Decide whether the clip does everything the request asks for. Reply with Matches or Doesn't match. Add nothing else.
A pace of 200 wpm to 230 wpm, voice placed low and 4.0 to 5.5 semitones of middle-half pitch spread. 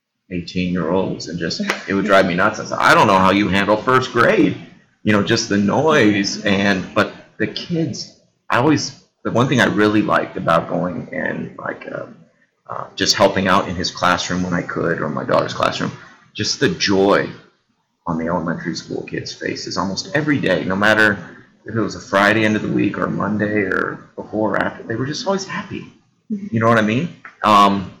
Doesn't match